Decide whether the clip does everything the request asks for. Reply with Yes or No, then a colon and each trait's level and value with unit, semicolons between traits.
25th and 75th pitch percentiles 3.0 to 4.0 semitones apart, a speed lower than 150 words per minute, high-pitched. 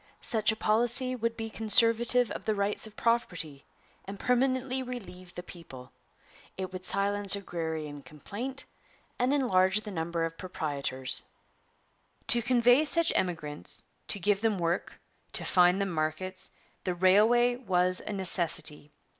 No: average, 5.3 semitones; average, 140 wpm; high, 200 Hz